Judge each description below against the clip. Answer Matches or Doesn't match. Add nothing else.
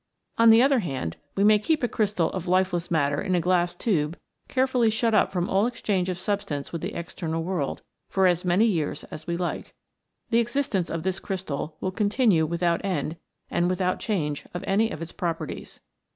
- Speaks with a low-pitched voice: Doesn't match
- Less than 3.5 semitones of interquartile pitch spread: Doesn't match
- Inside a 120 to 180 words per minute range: Doesn't match